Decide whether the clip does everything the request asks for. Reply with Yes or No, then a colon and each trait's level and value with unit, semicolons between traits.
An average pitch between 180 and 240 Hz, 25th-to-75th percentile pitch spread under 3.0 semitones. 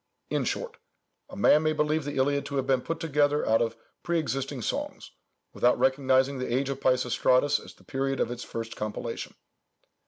No: low, 135 Hz; narrow, 2.4 semitones